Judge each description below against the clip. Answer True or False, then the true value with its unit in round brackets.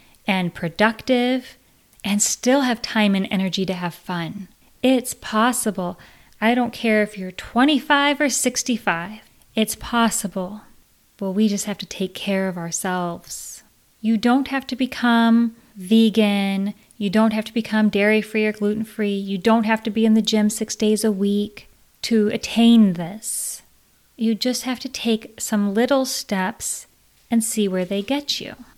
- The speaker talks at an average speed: True (160 wpm)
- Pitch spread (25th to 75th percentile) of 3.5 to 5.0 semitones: False (2.9 semitones)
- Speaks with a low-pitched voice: False (220 Hz)